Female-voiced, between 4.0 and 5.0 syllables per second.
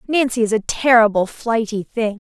Yes: female; 4.9 syllables/s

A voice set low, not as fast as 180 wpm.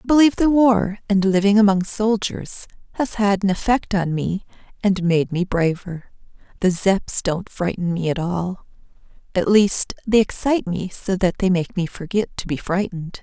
No: high, 195 Hz; average, 170 wpm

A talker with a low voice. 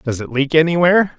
No: medium, 155 Hz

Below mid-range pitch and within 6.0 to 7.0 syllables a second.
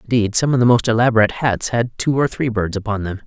Yes: low, 115 Hz; 6.6 syllables/s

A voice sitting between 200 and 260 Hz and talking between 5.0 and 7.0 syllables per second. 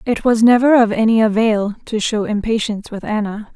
Yes: high, 220 Hz; 5.5 syllables/s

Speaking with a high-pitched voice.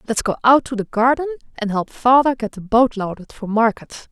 Yes: high, 235 Hz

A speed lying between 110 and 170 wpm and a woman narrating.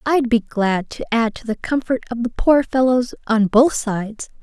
No: fast, 205 wpm; female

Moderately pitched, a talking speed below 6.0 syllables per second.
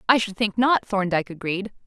No: high, 205 Hz; 5.7 syllables/s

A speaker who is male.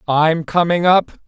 Yes: male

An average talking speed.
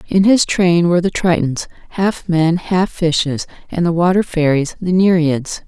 Yes: average, 170 wpm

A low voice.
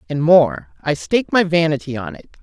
No: medium, 165 Hz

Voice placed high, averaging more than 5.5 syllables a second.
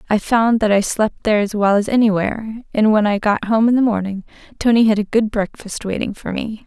Yes: high, 215 Hz; 5.8 syllables/s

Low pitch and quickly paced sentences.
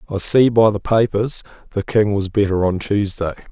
No: low, 105 Hz; average, 190 wpm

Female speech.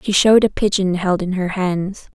Yes: female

